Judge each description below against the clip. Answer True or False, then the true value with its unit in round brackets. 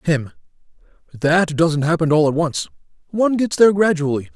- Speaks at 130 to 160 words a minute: True (140 wpm)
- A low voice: False (160 Hz)